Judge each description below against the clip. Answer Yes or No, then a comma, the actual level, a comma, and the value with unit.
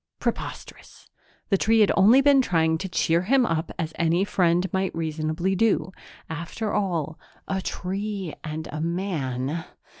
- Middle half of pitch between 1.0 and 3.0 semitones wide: No, average, 3.5 semitones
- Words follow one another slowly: No, average, 145 wpm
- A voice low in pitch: No, medium, 175 Hz